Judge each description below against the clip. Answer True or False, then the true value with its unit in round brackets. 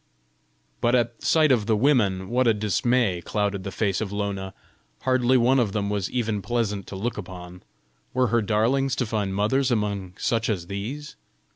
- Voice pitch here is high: False (110 Hz)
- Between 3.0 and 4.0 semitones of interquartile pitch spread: True (3.6 semitones)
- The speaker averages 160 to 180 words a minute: True (175 wpm)